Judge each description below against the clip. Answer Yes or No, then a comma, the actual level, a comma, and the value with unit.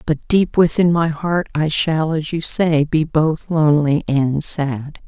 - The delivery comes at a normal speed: Yes, average, 175 wpm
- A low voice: No, medium, 155 Hz